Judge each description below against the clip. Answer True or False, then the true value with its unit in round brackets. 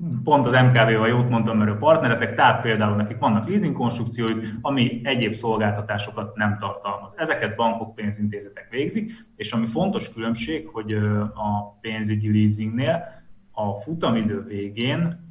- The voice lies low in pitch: True (115 Hz)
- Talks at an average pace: True (135 wpm)